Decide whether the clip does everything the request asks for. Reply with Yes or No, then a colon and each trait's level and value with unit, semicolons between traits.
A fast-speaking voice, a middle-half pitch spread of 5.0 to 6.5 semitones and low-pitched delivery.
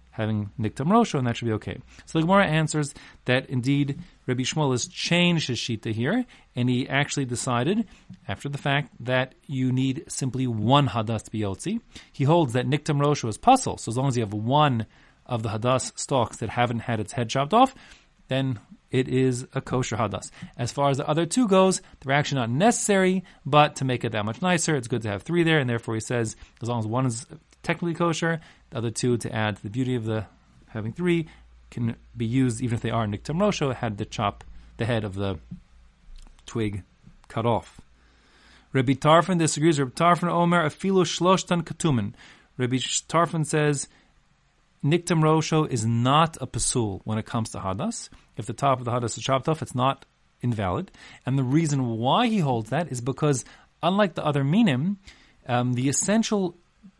No: average, 190 wpm; wide, 5.5 semitones; low, 130 Hz